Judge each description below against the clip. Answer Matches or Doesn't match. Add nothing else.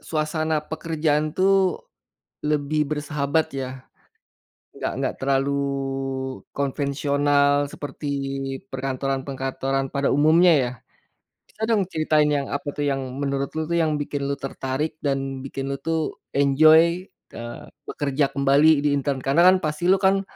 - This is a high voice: Doesn't match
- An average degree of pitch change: Doesn't match